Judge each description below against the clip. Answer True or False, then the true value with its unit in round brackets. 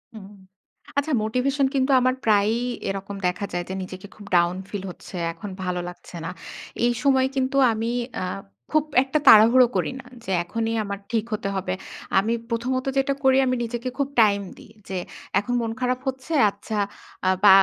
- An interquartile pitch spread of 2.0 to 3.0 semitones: False (4.4 semitones)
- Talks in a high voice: True (225 Hz)